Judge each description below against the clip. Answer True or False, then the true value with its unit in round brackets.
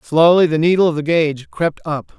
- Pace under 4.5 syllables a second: False (5.6 syllables/s)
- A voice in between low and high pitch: True (160 Hz)